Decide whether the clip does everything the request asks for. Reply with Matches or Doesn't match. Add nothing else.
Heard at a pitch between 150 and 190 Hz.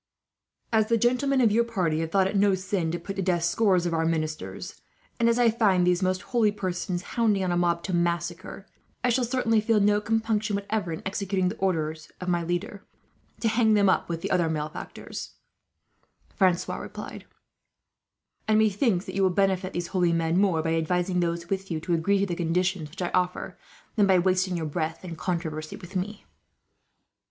Matches